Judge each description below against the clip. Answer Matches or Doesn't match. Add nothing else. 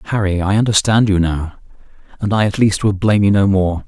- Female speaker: Doesn't match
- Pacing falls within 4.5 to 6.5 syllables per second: Matches